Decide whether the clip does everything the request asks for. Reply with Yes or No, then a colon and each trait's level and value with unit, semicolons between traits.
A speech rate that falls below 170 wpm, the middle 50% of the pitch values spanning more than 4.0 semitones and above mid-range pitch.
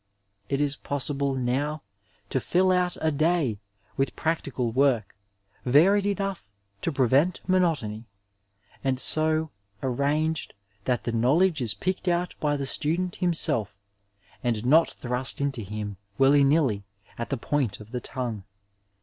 No: average, 140 wpm; average, 4.7 semitones; medium, 140 Hz